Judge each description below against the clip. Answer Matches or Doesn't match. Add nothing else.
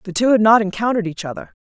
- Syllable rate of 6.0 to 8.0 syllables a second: Matches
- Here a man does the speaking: Doesn't match